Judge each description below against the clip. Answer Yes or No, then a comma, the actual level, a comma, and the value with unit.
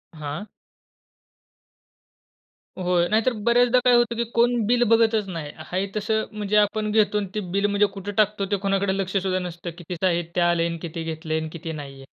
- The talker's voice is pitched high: Yes, high, 195 Hz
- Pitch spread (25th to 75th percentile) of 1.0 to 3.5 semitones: No, average, 4.0 semitones